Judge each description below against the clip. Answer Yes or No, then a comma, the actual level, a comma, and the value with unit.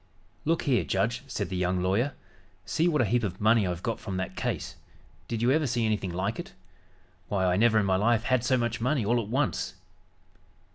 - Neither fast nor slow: No, fast, 210 wpm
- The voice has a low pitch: Yes, low, 115 Hz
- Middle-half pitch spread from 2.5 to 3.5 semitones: No, average, 4.5 semitones